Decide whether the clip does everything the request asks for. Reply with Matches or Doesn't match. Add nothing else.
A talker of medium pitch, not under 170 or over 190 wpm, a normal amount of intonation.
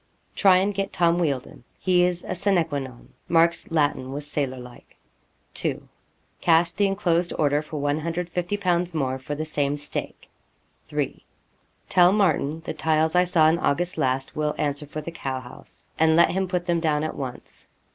Matches